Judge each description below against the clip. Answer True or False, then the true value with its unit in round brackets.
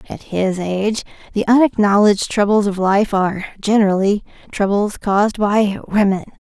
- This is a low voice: False (205 Hz)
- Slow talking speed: True (130 wpm)